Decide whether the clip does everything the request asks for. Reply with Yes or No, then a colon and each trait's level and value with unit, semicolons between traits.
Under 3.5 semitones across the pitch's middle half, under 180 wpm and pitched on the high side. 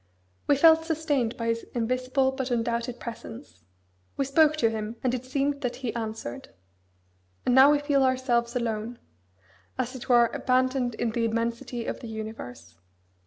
Yes: narrow, 2.5 semitones; average, 160 wpm; high, 245 Hz